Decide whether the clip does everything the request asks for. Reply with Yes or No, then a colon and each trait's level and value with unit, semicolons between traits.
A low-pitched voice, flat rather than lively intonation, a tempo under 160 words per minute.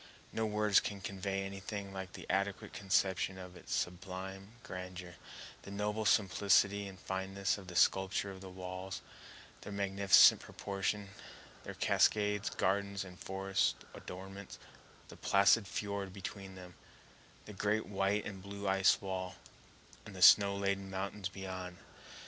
Yes: very low, 95 Hz; narrow, 1.1 semitones; slow, 135 wpm